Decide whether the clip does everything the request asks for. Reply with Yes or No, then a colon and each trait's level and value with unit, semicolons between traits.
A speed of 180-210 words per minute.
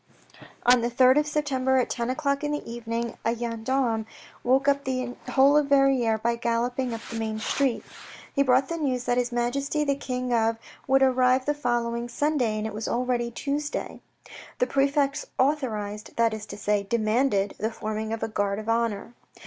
Yes: average, 185 wpm